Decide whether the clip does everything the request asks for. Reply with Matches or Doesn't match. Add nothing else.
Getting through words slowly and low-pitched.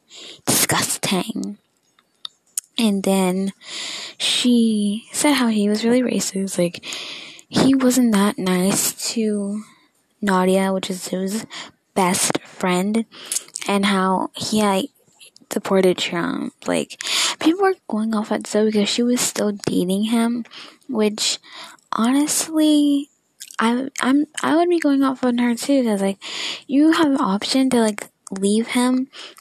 Doesn't match